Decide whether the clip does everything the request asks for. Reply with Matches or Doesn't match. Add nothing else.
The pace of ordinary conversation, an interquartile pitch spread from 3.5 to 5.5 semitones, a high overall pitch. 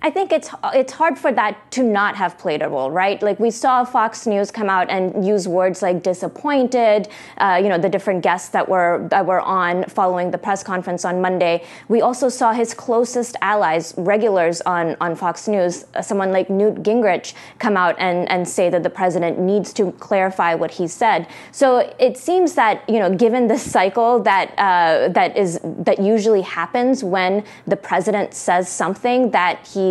Matches